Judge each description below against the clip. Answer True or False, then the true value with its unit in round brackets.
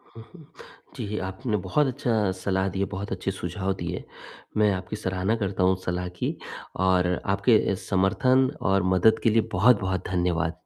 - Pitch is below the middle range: True (95 Hz)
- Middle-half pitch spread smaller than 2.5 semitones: False (2.9 semitones)